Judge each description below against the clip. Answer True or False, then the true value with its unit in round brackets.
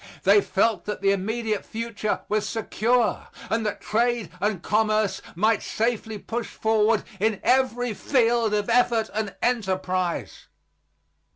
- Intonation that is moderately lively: False (2.1 semitones)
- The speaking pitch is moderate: False (220 Hz)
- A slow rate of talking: True (125 wpm)